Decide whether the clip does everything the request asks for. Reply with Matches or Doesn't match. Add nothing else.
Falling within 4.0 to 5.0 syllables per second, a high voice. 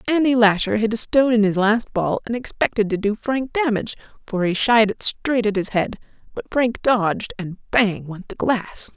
Matches